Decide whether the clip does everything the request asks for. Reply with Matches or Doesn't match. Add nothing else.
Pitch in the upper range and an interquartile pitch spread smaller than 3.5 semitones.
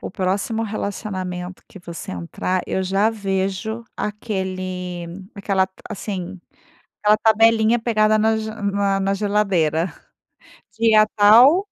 Matches